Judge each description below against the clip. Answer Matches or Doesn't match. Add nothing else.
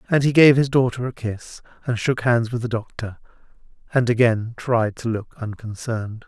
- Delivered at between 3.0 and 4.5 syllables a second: Doesn't match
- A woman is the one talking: Doesn't match